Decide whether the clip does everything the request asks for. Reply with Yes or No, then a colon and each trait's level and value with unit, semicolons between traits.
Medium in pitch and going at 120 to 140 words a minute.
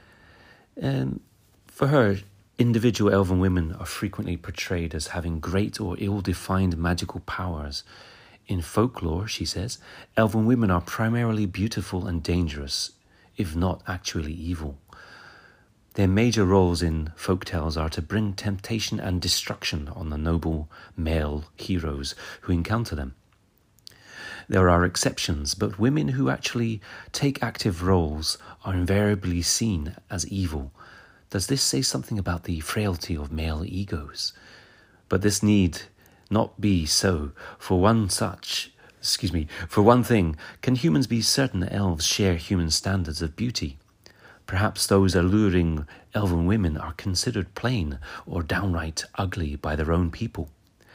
No: very low, 95 Hz; slow, 135 wpm